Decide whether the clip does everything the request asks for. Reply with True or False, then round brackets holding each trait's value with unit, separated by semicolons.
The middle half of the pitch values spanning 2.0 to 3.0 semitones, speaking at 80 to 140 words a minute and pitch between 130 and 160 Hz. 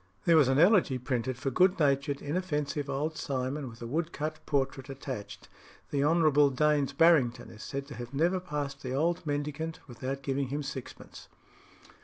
False (2.7 semitones; 165 wpm; 140 Hz)